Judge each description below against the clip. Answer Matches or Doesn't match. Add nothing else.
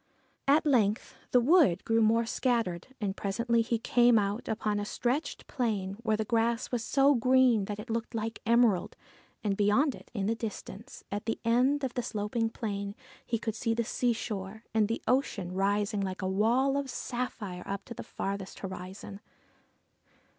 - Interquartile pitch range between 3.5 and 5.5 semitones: Doesn't match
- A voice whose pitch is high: Matches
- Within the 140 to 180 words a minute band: Matches